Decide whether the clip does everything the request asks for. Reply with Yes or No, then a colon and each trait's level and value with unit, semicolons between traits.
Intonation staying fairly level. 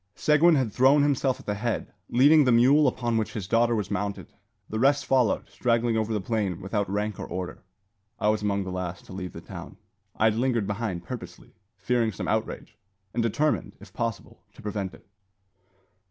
No: average, 3.5 semitones